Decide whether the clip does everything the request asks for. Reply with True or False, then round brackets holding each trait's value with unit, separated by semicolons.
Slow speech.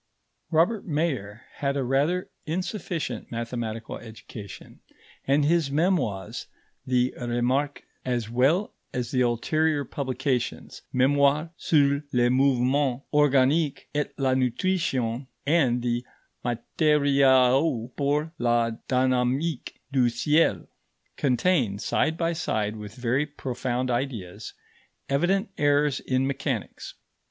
True (105 wpm)